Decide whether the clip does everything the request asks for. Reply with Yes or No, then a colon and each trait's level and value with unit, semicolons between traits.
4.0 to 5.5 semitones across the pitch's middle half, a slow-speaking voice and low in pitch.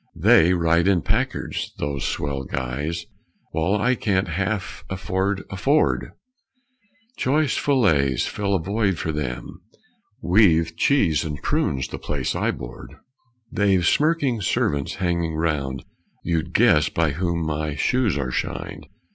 Yes: average, 4.8 semitones; slow, 130 wpm; very low, 85 Hz